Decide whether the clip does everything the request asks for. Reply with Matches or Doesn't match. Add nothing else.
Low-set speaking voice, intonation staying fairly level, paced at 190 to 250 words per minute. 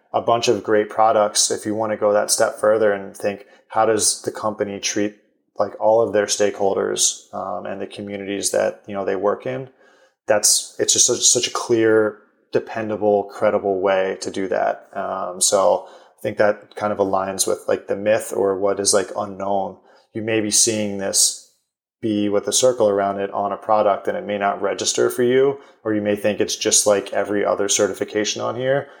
Matches